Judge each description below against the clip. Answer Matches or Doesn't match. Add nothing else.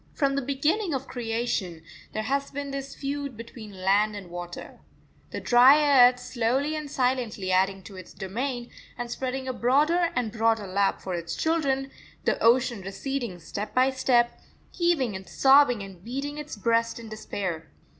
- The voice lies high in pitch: Matches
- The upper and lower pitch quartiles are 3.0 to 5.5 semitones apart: Matches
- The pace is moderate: Matches